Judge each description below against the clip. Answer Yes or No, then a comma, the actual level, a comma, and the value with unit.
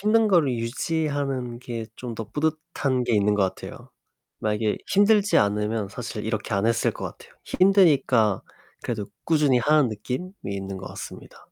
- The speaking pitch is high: No, low, 125 Hz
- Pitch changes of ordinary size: No, wide, 6.4 semitones